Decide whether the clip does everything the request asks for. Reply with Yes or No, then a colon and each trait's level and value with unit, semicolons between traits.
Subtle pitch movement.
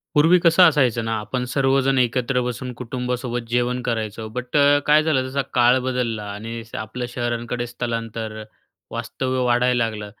Yes: narrow, 1.9 semitones